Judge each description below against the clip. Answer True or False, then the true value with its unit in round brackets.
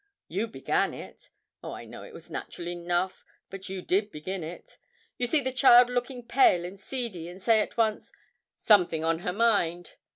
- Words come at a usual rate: True (185 wpm)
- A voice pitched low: False (195 Hz)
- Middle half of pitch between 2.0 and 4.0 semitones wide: False (5.1 semitones)